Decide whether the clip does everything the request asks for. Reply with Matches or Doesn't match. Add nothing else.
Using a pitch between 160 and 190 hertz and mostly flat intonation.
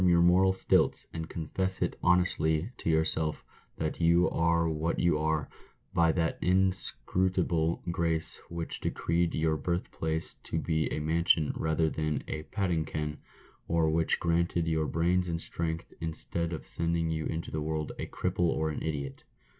Doesn't match